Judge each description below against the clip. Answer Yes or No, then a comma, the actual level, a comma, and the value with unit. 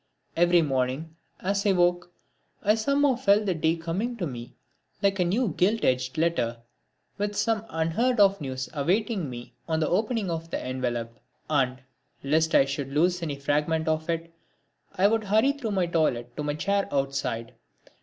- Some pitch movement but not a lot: No, wide, 6.3 semitones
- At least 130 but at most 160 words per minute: No, average, 170 wpm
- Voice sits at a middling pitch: Yes, medium, 165 Hz